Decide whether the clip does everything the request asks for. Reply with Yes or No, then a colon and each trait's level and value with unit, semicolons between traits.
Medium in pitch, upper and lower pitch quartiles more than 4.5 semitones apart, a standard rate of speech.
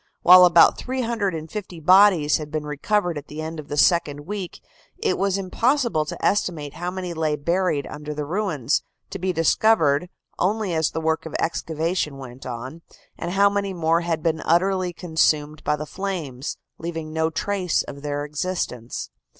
No: medium, 165 Hz; average, 3.8 semitones; average, 165 wpm